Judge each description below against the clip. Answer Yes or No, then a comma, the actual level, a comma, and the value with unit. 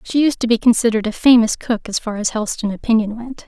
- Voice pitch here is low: No, high, 225 Hz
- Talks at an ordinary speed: No, fast, 240 wpm